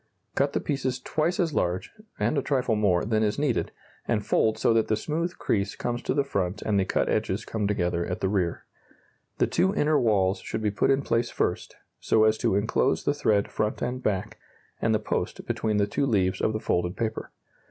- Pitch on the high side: No, low, 110 Hz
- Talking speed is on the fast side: Yes, fast, 215 wpm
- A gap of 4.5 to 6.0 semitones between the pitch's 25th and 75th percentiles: Yes, average, 5.0 semitones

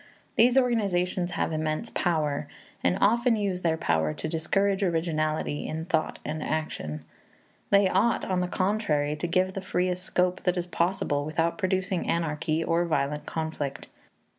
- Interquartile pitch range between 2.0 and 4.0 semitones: Yes, average, 3.3 semitones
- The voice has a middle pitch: Yes, medium, 175 Hz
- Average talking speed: Yes, average, 150 wpm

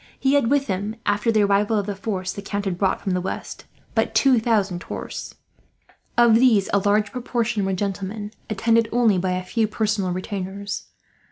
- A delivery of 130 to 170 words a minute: No, average, 185 wpm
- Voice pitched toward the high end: Yes, high, 205 Hz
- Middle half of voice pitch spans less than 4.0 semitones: Yes, average, 2.7 semitones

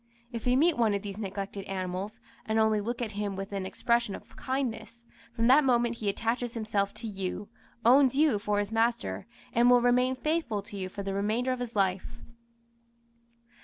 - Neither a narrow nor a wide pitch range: Yes, average, 3.4 semitones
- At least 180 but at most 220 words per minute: Yes, average, 190 wpm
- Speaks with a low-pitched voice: No, high, 220 Hz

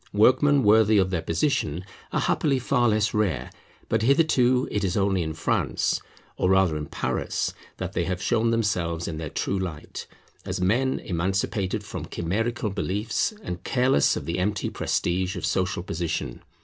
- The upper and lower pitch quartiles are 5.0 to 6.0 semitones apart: No, average, 4.6 semitones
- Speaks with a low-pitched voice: Yes, very low, 95 Hz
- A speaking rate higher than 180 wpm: No, average, 160 wpm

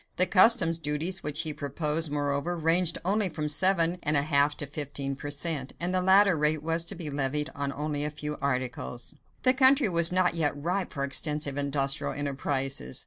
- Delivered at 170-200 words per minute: Yes, average, 190 wpm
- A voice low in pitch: No, medium, 150 Hz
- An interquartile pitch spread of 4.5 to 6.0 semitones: No, average, 3.3 semitones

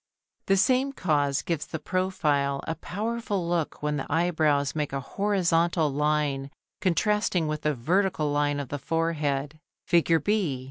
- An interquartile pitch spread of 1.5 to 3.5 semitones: No, average, 4.1 semitones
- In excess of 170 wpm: No, average, 145 wpm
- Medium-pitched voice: Yes, medium, 160 Hz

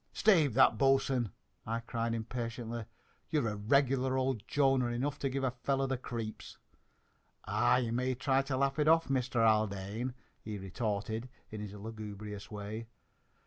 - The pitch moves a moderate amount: Yes, average, 3.6 semitones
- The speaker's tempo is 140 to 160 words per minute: Yes, average, 155 wpm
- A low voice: Yes, low, 120 Hz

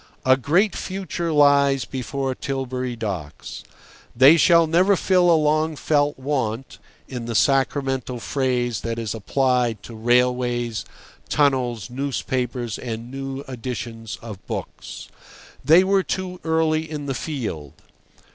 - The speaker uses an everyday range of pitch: Yes, average, 3.9 semitones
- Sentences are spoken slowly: Yes, slow, 125 wpm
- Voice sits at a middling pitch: No, low, 130 Hz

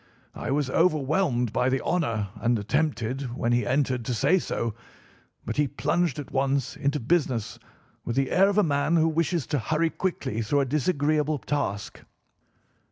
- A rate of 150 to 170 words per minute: Yes, average, 165 wpm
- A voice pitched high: No, medium, 140 Hz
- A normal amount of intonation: Yes, average, 4.3 semitones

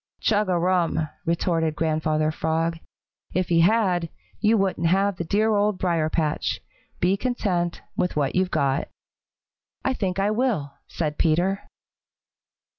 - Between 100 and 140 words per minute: Yes, slow, 135 wpm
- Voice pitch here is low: No, medium, 175 Hz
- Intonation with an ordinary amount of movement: Yes, average, 3.6 semitones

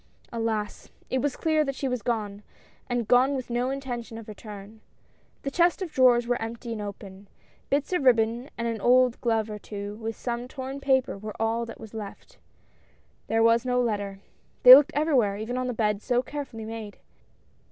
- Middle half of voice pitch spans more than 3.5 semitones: No, average, 2.9 semitones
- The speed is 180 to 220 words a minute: Yes, average, 185 wpm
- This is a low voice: No, high, 235 Hz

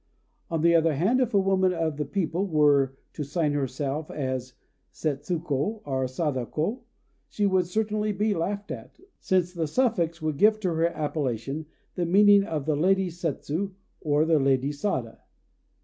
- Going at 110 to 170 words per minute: Yes, average, 160 wpm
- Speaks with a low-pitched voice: No, medium, 165 Hz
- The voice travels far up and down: No, average, 4.8 semitones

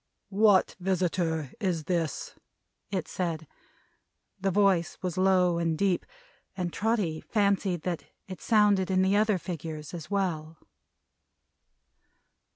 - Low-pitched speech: No, medium, 185 Hz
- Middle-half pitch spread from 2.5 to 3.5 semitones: Yes, average, 2.8 semitones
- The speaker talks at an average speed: No, slow, 115 wpm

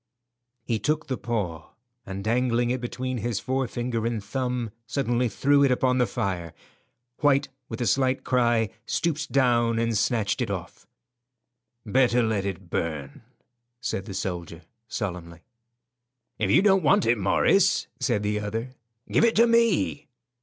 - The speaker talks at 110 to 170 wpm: Yes, average, 145 wpm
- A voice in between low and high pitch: No, low, 120 Hz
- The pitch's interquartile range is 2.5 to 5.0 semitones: Yes, average, 4.3 semitones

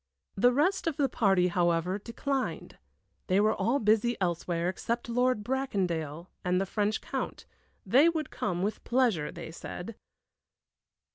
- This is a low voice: No, high, 210 Hz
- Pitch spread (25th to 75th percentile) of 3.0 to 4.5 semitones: No, wide, 5.6 semitones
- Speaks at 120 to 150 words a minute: Yes, average, 140 wpm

